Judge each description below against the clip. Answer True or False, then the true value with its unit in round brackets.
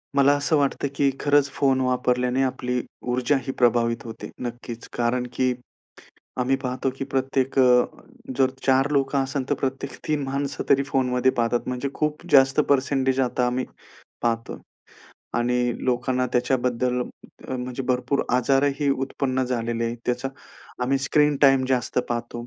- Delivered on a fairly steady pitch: True (1.8 semitones)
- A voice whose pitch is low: True (130 Hz)